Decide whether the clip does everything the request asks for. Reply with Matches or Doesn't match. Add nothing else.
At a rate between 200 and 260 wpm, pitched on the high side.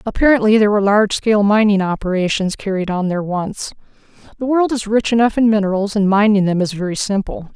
Doesn't match